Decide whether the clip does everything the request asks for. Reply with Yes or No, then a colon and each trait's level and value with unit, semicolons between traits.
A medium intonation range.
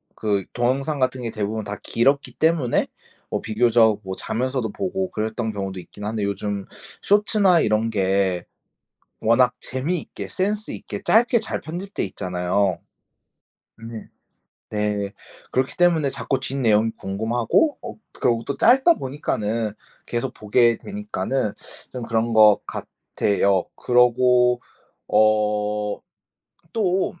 Yes: average, 4.8 semitones